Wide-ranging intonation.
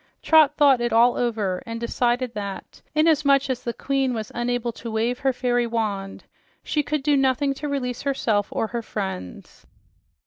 No: average, 3.3 semitones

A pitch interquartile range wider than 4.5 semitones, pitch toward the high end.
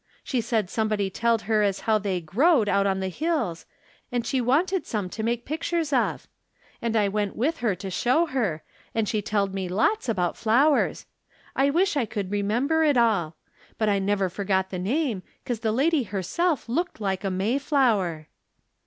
Yes: wide, 5.5 semitones; high, 220 Hz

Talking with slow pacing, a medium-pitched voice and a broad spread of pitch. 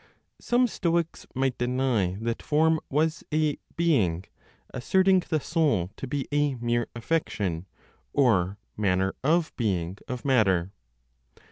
No: slow, 120 wpm; low, 130 Hz; wide, 7.8 semitones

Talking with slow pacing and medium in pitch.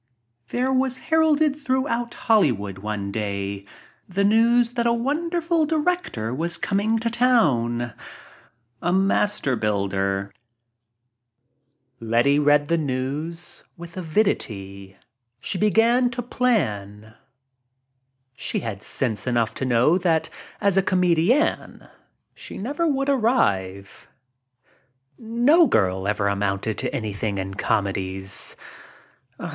Yes: slow, 110 wpm; medium, 160 Hz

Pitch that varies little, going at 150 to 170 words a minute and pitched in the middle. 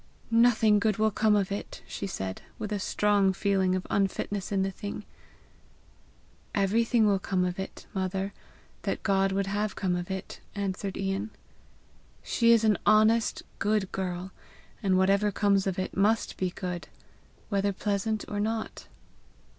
No: narrow, 1.8 semitones; average, 155 wpm; high, 200 Hz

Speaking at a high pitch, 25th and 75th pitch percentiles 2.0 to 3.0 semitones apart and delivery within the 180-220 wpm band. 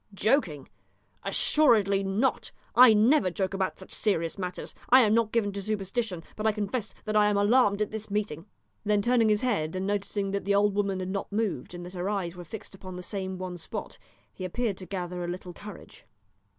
Yes: high, 200 Hz; narrow, 2.5 semitones; fast, 205 wpm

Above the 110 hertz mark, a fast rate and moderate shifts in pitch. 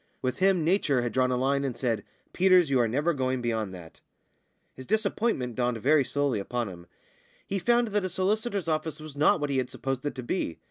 No: medium, 140 Hz; fast, 215 wpm; wide, 6.6 semitones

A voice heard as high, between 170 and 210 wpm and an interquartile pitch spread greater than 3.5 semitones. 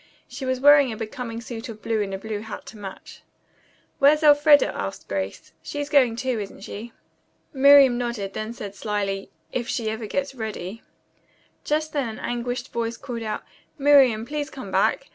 Yes: high, 235 Hz; average, 175 wpm; average, 4.3 semitones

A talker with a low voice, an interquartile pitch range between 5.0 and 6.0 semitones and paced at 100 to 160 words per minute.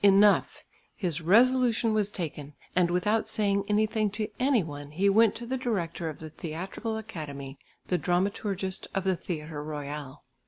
No: high, 190 Hz; wide, 5.4 semitones; average, 155 wpm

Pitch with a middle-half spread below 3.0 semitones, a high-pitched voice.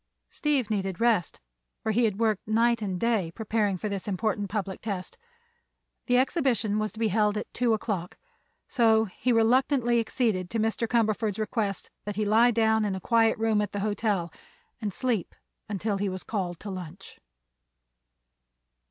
Yes: narrow, 2.5 semitones; high, 215 Hz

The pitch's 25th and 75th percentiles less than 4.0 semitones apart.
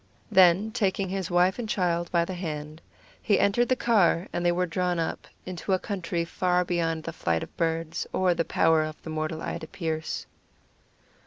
Yes: narrow, 2.5 semitones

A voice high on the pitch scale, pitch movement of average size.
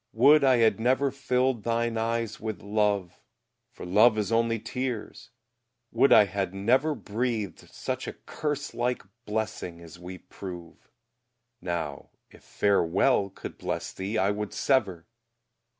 No: low, 110 Hz; average, 4.0 semitones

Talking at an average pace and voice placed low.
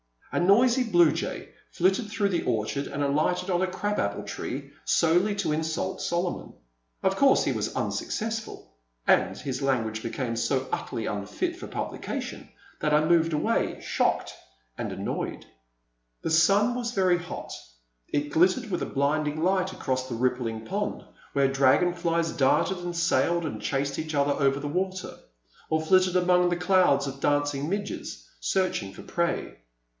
No: average, 160 wpm; medium, 165 Hz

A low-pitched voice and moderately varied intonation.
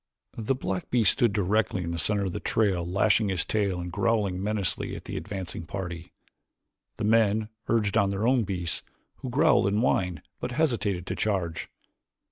Yes: low, 100 Hz; average, 3.3 semitones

